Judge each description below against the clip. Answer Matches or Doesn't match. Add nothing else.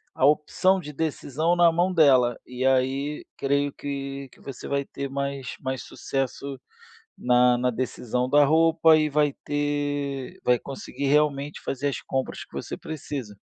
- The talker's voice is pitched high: Doesn't match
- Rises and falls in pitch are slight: Matches